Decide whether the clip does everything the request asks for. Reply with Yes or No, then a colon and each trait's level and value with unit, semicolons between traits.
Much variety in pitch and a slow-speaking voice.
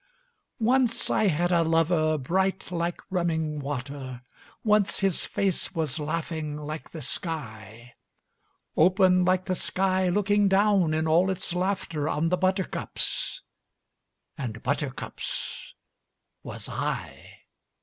No: average, 3.8 semitones; slow, 115 wpm